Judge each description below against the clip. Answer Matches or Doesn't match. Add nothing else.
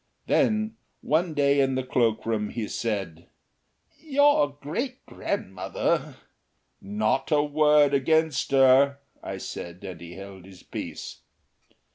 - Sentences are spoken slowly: Matches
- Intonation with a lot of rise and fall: Matches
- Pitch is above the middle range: Doesn't match